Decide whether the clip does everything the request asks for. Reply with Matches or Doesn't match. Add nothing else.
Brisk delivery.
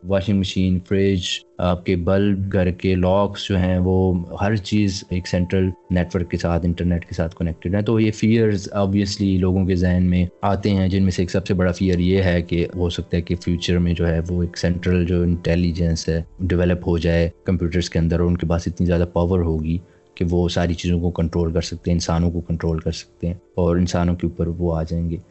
Matches